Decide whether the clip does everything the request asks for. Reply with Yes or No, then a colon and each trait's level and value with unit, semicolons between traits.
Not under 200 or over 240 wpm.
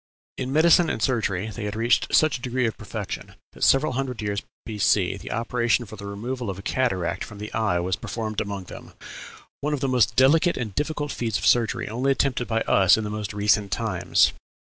Yes: fast, 205 wpm